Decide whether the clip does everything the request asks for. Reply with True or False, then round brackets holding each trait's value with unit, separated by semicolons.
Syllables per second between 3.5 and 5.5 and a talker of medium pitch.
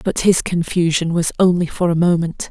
True (5.1 syllables/s; 170 Hz)